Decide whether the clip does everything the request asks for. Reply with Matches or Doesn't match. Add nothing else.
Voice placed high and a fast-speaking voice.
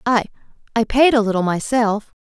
Doesn't match